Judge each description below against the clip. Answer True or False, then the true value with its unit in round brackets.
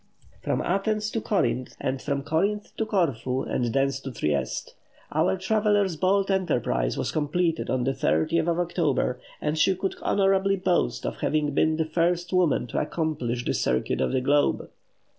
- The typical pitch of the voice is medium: True (160 Hz)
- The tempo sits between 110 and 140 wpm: False (165 wpm)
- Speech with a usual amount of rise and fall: False (6.0 semitones)